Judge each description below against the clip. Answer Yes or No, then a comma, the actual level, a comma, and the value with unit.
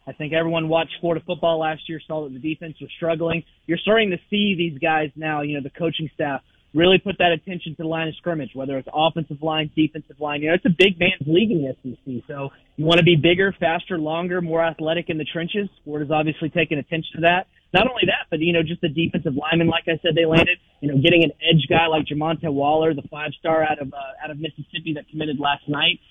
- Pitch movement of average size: No, narrow, 1.8 semitones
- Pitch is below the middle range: No, medium, 160 Hz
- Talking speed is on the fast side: Yes, fast, 245 wpm